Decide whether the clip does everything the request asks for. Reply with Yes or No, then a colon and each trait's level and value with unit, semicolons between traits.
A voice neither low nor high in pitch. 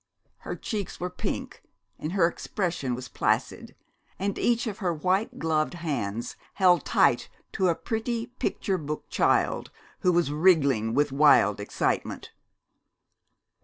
Yes: medium, 170 Hz